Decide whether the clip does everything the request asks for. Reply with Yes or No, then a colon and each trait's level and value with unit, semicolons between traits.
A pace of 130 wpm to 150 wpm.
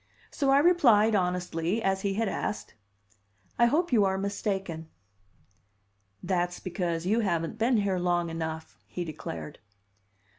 Yes: slow, 135 wpm